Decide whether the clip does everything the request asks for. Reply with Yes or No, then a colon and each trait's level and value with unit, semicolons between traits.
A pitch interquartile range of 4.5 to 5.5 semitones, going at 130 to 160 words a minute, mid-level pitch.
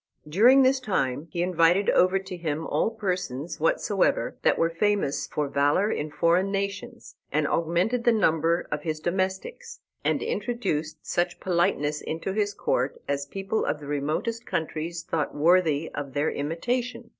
Yes: average, 5.0 semitones; average, 155 wpm; medium, 170 Hz